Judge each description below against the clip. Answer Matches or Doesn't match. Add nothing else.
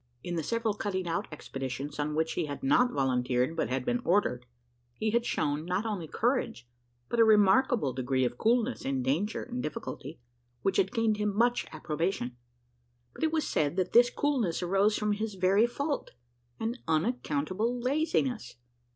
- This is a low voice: Doesn't match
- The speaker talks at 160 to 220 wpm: Matches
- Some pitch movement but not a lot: Doesn't match